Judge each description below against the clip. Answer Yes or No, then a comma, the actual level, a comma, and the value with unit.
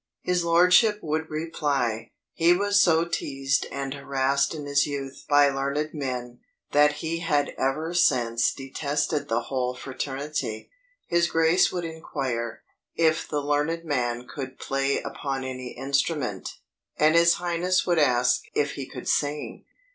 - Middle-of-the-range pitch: Yes, medium, 145 Hz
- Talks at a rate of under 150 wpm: Yes, average, 140 wpm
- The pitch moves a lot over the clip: No, average, 3.4 semitones